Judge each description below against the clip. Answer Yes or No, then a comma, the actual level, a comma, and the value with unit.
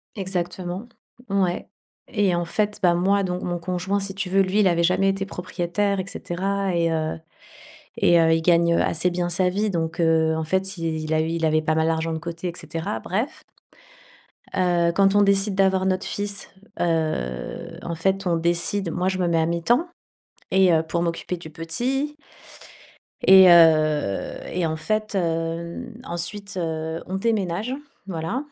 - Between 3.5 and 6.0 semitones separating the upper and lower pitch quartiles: No, average, 2.8 semitones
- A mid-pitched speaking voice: Yes, medium, 175 Hz